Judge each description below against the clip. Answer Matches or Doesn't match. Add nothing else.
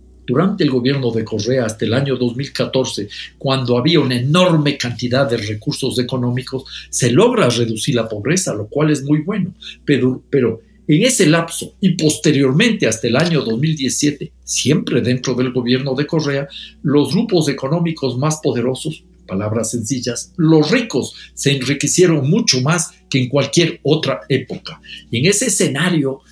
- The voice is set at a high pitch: Doesn't match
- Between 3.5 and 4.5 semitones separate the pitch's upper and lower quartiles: Matches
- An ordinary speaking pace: Matches